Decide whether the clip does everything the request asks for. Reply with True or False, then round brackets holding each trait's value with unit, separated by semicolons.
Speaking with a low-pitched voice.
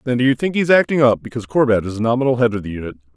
True (120 Hz)